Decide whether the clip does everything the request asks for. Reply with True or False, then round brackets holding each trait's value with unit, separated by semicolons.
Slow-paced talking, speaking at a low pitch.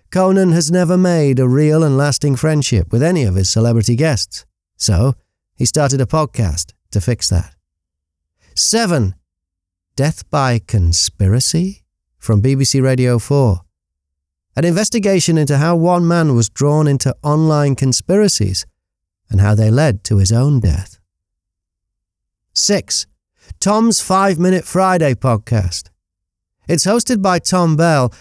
True (130 wpm; 125 Hz)